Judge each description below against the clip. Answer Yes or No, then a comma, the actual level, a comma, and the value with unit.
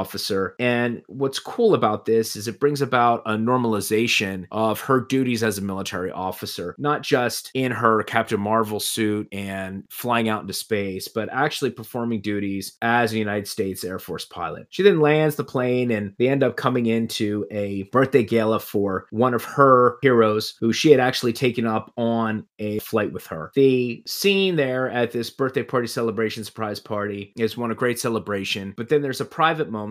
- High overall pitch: No, low, 115 Hz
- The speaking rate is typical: Yes, average, 185 wpm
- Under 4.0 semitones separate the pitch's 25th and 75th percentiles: Yes, average, 3.2 semitones